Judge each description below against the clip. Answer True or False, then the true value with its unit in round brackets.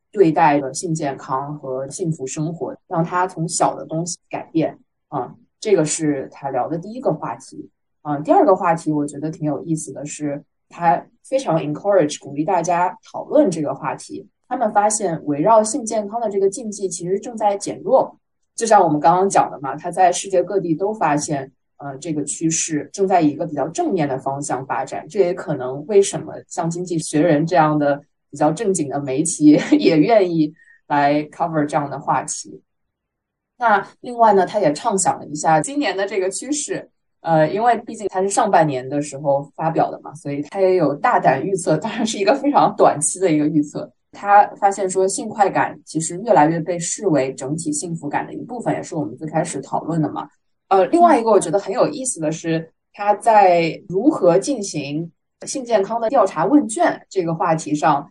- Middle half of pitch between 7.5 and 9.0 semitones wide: False (5.1 semitones)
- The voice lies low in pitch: False (170 Hz)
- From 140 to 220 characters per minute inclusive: False (300 characters per minute)